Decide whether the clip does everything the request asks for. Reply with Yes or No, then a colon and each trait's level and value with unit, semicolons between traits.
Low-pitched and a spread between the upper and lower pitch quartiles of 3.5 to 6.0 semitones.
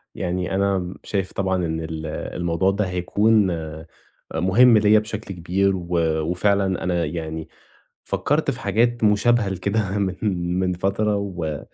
No: very low, 95 Hz; average, 2.9 semitones